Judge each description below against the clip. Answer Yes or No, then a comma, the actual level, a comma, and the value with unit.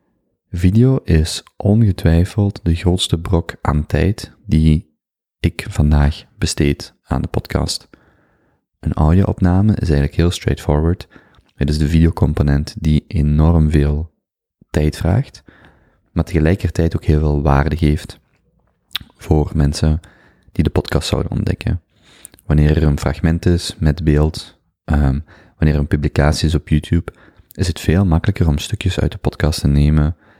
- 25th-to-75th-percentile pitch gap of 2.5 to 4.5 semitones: Yes, average, 3.6 semitones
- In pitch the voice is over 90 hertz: No, very low, 80 Hz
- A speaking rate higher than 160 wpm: No, slow, 135 wpm